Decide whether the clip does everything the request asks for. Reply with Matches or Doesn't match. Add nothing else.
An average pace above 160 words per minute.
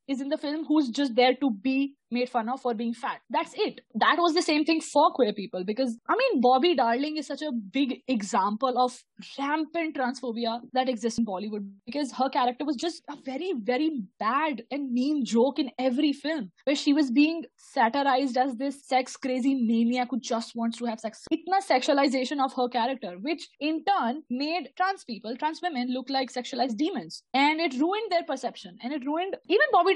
Matches